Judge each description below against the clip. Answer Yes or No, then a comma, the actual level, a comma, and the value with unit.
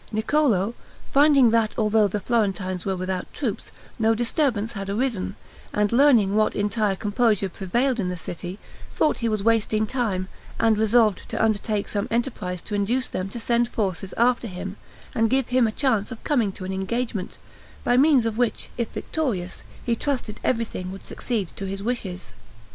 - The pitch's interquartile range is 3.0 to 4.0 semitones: Yes, average, 3.6 semitones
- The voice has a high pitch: Yes, high, 220 Hz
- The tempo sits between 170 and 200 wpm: Yes, average, 175 wpm